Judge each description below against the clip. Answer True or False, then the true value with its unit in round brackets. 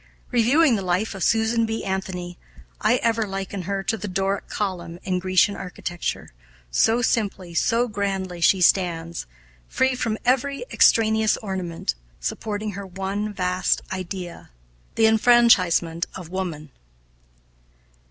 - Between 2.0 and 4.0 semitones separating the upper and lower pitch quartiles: True (3.5 semitones)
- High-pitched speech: True (195 Hz)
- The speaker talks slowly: True (125 wpm)